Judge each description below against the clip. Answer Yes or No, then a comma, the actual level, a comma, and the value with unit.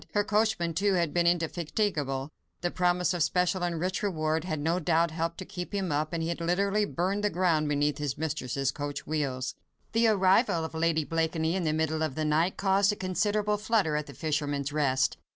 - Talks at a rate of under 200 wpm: No, fast, 205 wpm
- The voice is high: No, medium, 165 Hz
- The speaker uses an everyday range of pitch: Yes, average, 3.5 semitones